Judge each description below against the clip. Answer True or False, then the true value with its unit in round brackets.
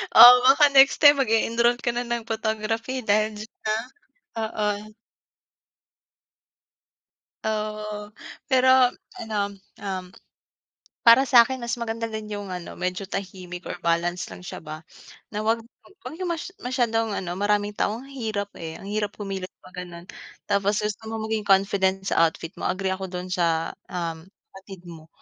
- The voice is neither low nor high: False (210 Hz)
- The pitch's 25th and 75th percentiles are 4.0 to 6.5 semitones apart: False (3.5 semitones)